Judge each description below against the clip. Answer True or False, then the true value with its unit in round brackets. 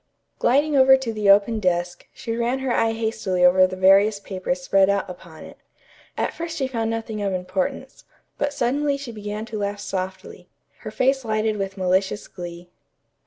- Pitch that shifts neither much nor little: True (4.0 semitones)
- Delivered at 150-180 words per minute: True (175 wpm)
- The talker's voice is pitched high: True (210 Hz)